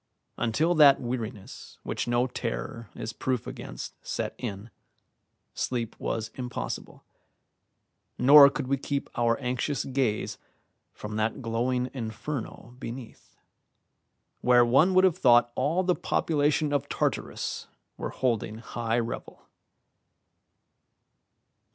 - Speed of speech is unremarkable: No, slow, 110 wpm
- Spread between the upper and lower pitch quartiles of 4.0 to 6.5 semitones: No, average, 3.4 semitones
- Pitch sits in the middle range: No, low, 125 Hz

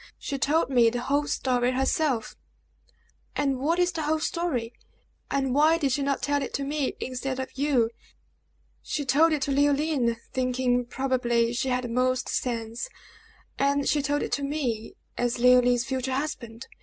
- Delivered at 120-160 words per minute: No, average, 170 wpm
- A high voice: Yes, very high, 265 Hz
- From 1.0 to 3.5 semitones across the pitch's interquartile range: Yes, average, 2.7 semitones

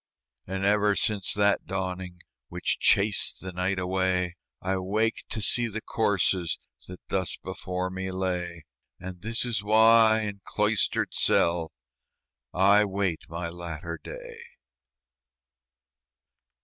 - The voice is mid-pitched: No, very low, 95 Hz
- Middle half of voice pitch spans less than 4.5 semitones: Yes, narrow, 2.4 semitones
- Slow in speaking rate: Yes, slow, 120 wpm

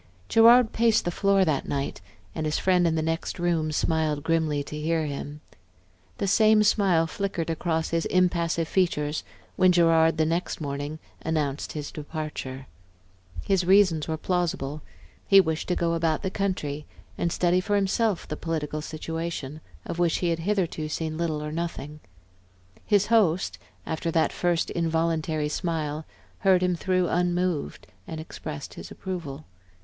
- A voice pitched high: No, medium, 165 Hz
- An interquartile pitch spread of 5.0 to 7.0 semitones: No, average, 2.9 semitones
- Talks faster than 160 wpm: No, average, 155 wpm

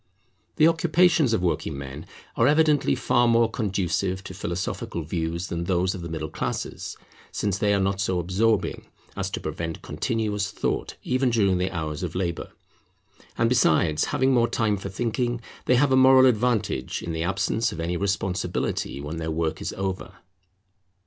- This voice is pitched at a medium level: No, very low, 95 Hz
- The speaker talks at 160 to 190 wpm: Yes, average, 170 wpm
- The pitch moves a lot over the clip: Yes, wide, 5.7 semitones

